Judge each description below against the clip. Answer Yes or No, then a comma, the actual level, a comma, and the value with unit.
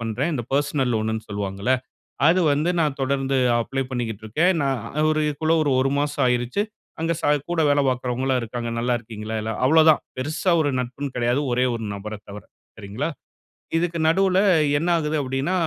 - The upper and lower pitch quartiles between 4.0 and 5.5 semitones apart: Yes, average, 4.4 semitones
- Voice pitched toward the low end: Yes, low, 130 Hz